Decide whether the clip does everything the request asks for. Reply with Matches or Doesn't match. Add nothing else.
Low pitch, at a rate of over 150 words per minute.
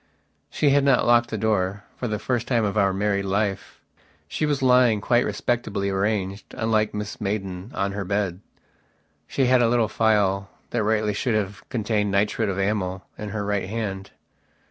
Matches